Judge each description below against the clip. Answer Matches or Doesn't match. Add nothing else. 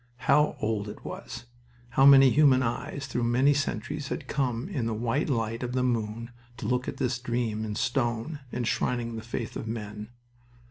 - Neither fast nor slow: Matches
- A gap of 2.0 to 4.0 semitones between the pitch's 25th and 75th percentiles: Matches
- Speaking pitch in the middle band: Doesn't match